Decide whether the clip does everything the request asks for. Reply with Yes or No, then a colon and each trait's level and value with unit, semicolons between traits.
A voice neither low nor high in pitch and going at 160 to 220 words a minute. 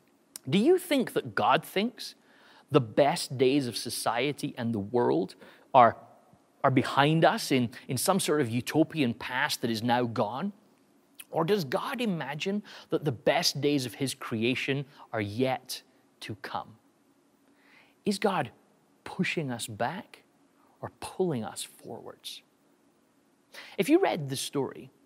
No: medium, 145 Hz; average, 140 wpm